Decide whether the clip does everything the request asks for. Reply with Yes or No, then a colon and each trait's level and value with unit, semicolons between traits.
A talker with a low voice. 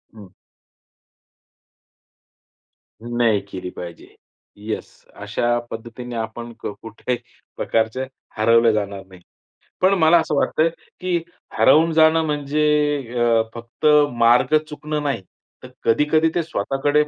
Yes: low, 120 Hz